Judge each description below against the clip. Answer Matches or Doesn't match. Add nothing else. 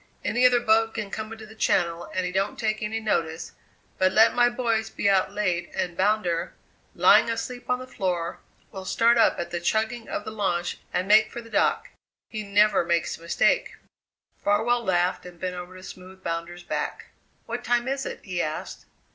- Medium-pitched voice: Doesn't match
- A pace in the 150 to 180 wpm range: Doesn't match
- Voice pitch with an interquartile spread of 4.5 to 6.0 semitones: Doesn't match